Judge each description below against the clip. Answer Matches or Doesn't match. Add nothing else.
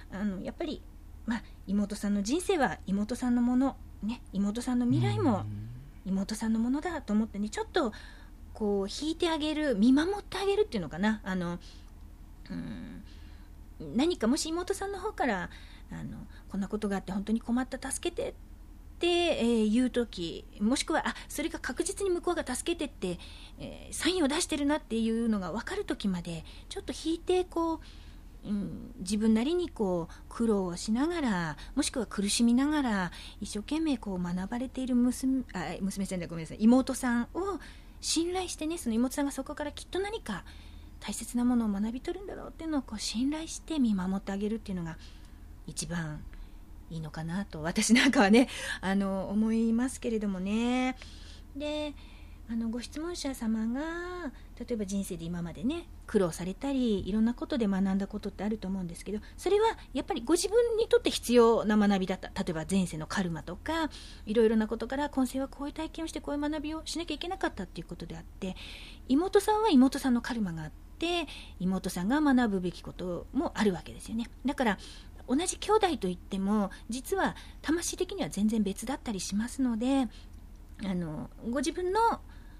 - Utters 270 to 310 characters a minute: Doesn't match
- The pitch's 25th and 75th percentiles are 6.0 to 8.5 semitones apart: Matches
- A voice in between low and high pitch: Doesn't match